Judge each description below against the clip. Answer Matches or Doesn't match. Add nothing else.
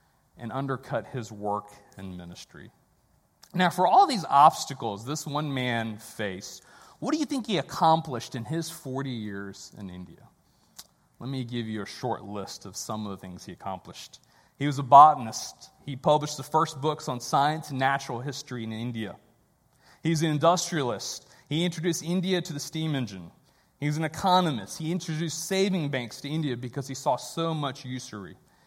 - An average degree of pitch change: Doesn't match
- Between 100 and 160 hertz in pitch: Matches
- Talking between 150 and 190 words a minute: Matches